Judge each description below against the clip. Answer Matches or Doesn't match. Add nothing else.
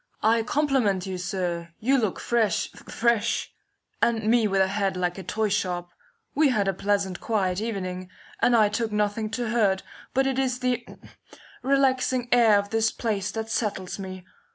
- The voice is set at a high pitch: Matches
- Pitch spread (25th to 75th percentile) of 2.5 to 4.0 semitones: Matches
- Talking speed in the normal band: Matches